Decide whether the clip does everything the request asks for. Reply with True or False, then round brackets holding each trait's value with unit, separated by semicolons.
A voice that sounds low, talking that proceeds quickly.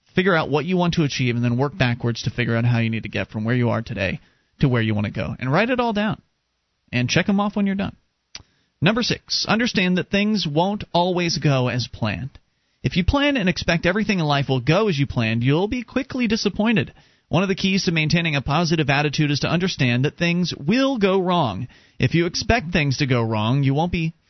False (160 Hz; 235 wpm)